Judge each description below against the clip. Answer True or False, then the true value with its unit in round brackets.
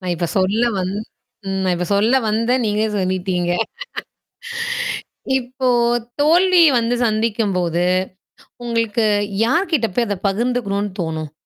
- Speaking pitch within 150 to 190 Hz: False (215 Hz)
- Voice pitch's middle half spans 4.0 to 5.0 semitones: True (4.5 semitones)